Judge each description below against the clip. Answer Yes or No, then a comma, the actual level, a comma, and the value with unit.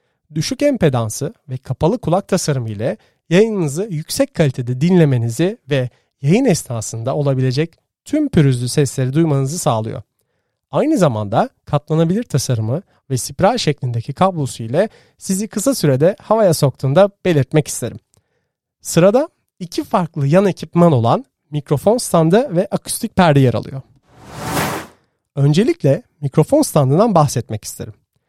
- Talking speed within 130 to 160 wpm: No, average, 115 wpm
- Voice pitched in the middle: Yes, medium, 150 Hz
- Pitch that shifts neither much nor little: No, wide, 6.0 semitones